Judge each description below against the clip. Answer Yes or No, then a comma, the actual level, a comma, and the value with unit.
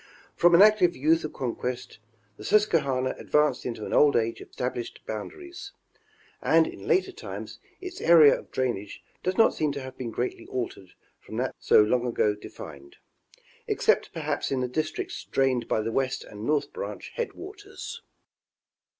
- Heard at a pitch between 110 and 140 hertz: Yes, low, 135 Hz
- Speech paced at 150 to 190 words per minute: Yes, average, 165 wpm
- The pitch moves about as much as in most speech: No, wide, 6.7 semitones